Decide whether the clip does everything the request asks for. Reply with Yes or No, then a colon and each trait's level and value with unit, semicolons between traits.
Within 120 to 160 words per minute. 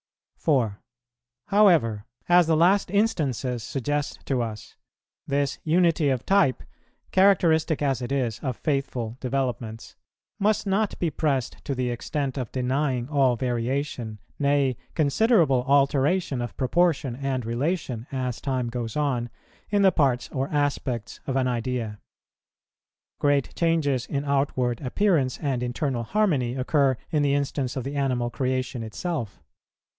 Yes: slow, 135 wpm